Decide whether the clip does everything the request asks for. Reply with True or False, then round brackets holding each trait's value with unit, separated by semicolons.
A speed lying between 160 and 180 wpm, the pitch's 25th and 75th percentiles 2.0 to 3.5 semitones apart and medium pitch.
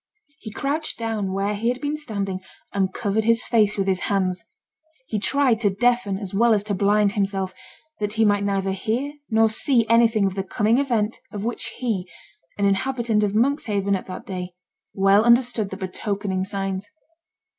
False (175 wpm; 2.9 semitones; 210 Hz)